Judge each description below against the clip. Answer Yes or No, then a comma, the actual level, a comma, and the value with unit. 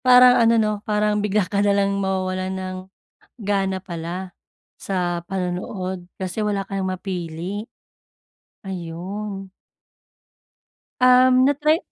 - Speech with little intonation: Yes, narrow, 2.2 semitones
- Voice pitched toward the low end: No, high, 195 Hz